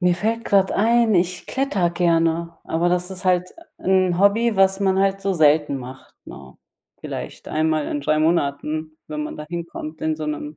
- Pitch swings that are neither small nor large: Yes, average, 3.7 semitones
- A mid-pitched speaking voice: Yes, medium, 175 Hz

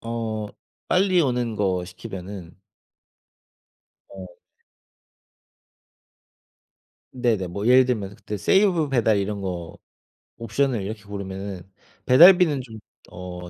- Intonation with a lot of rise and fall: No, average, 4.7 semitones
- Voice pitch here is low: Yes, low, 105 Hz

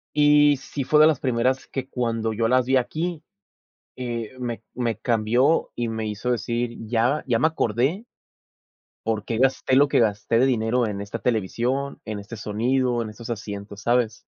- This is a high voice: No, low, 120 Hz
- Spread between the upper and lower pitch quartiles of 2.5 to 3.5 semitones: Yes, average, 2.9 semitones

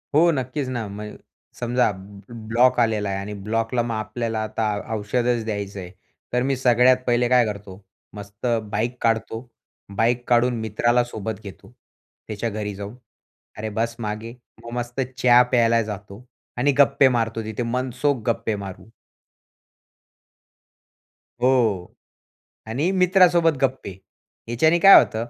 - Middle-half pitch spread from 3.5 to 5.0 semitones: No, average, 2.7 semitones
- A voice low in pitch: Yes, low, 115 Hz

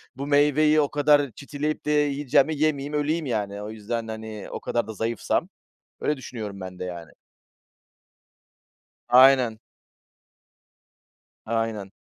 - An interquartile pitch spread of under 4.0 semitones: No, average, 5.1 semitones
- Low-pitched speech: Yes, low, 130 Hz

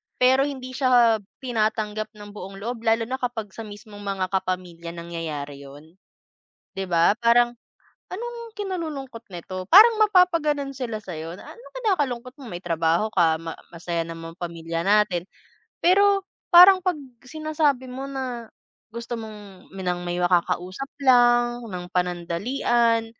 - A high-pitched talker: Yes, high, 220 Hz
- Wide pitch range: Yes, wide, 6.7 semitones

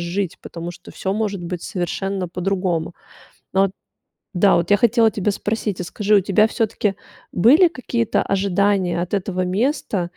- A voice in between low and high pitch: No, high, 195 Hz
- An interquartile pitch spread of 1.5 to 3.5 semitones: Yes, average, 2.9 semitones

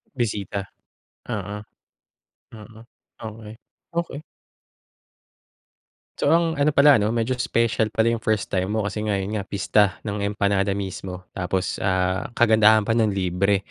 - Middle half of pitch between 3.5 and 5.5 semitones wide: No, narrow, 2.4 semitones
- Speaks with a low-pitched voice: Yes, low, 105 Hz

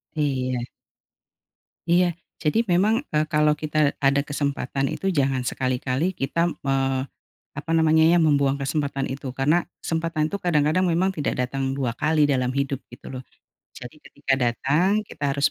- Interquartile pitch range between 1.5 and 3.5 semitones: Yes, average, 2.8 semitones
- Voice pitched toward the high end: No, medium, 145 Hz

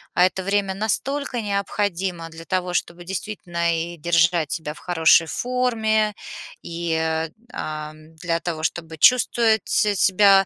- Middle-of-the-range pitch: Yes, medium, 180 Hz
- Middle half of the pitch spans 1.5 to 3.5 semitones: No, average, 3.9 semitones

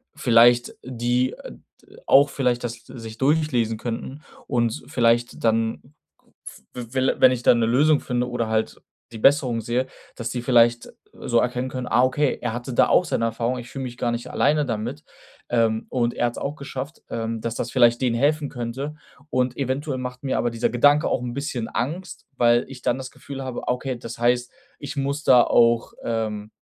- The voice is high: No, low, 120 Hz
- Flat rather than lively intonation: Yes, narrow, 2.2 semitones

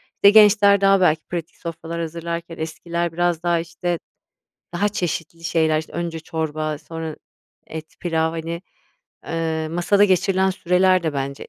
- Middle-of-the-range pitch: Yes, medium, 170 Hz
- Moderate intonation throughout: No, narrow, 1.8 semitones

